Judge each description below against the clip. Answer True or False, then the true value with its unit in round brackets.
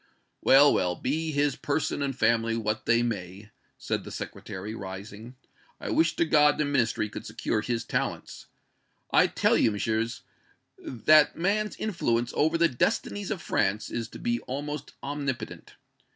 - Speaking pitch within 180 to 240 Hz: False (120 Hz)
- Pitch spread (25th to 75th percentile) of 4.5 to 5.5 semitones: True (5.2 semitones)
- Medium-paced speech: True (150 wpm)